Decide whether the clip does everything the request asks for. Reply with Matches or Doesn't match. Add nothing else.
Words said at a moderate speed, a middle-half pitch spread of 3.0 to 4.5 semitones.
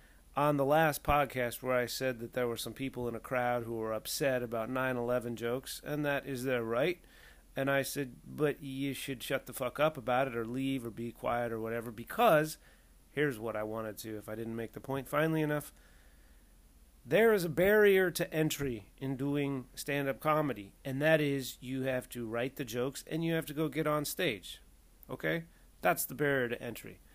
Doesn't match